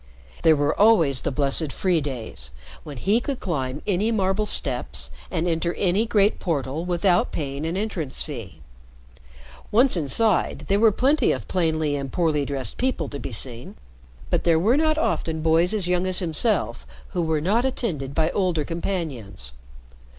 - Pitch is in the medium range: Yes, medium, 165 Hz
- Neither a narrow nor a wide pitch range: No, wide, 6.0 semitones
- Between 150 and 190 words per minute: Yes, average, 165 wpm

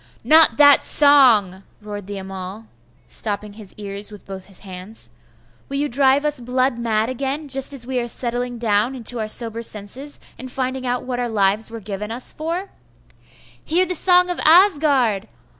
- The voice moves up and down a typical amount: Yes, average, 4.8 semitones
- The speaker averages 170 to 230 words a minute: Yes, average, 175 wpm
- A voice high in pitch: Yes, high, 240 Hz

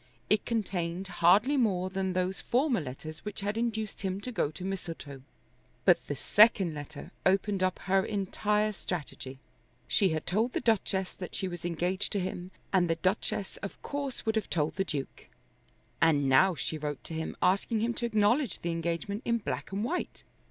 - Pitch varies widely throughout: No, average, 4.0 semitones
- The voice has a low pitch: No, high, 190 Hz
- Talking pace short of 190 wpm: Yes, average, 180 wpm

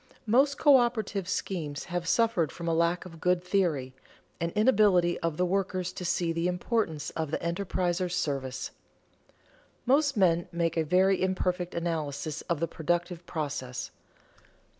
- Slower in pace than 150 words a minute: Yes, average, 140 wpm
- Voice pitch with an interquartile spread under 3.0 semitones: Yes, narrow, 2.4 semitones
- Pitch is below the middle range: No, medium, 175 Hz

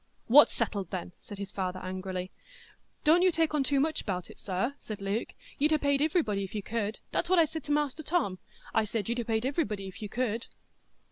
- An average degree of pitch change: No, wide, 7.1 semitones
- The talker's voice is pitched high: Yes, high, 230 Hz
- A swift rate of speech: Yes, fast, 210 wpm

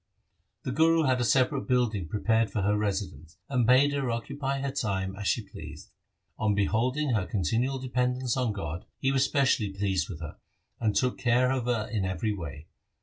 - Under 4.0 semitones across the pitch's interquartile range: No, average, 4.7 semitones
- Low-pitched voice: Yes, low, 115 Hz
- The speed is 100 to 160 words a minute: No, average, 185 wpm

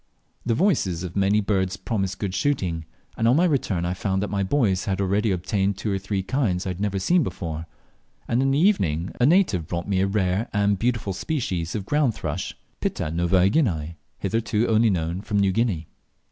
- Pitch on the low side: Yes, low, 100 Hz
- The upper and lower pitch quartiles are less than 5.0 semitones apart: Yes, average, 3.9 semitones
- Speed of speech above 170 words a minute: Yes, average, 195 wpm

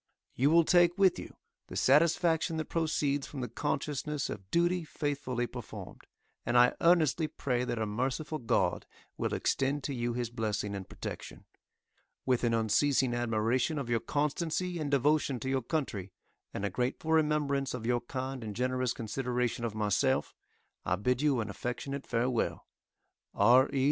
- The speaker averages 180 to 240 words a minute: No, average, 160 wpm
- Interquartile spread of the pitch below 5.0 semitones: Yes, average, 4.1 semitones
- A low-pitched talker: Yes, low, 130 Hz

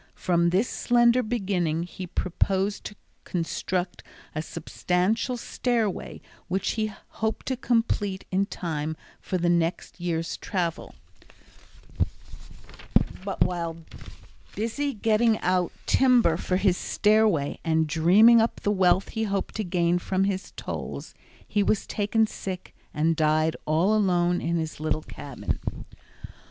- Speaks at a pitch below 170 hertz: No, medium, 185 Hz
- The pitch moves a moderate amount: Yes, average, 4.2 semitones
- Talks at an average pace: No, slow, 125 wpm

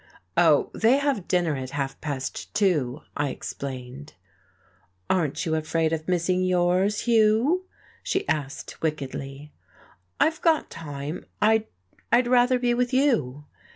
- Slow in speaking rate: Yes, slow, 125 wpm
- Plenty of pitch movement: Yes, wide, 8.5 semitones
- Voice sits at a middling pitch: Yes, medium, 175 Hz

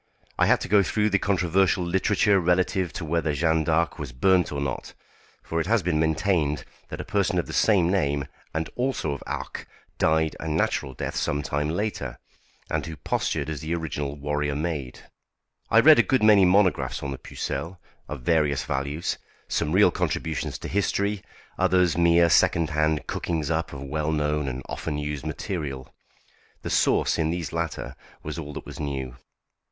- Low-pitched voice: Yes, very low, 80 Hz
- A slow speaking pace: No, average, 180 wpm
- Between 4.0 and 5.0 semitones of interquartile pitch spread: No, average, 3.6 semitones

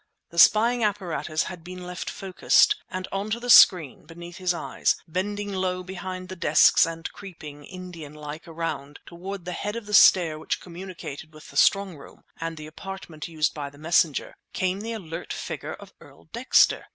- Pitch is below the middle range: No, medium, 180 Hz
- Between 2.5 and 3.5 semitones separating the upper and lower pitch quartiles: Yes, average, 3.2 semitones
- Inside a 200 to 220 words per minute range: No, average, 175 wpm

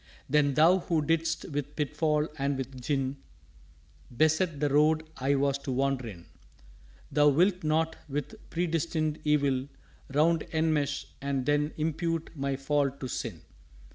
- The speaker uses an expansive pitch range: No, narrow, 2.4 semitones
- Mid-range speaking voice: Yes, medium, 145 Hz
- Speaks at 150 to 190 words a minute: No, average, 140 wpm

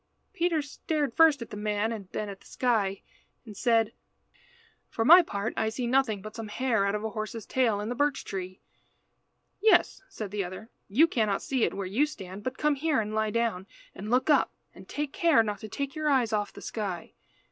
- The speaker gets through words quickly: Yes, fast, 210 wpm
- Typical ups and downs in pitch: Yes, average, 4.9 semitones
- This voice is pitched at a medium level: No, high, 225 Hz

